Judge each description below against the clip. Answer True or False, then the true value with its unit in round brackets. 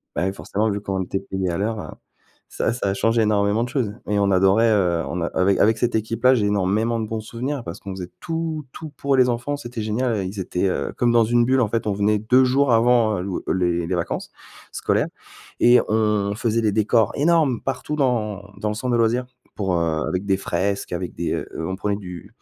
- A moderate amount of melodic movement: True (3.6 semitones)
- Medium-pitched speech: False (110 Hz)